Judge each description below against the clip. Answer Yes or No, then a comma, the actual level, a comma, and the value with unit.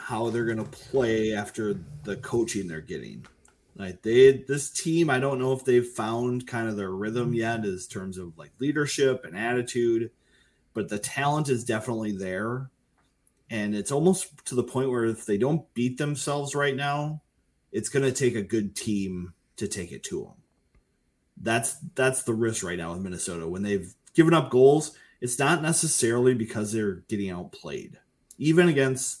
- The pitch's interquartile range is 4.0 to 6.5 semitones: Yes, average, 4.6 semitones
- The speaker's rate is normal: Yes, average, 175 wpm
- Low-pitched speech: Yes, low, 120 Hz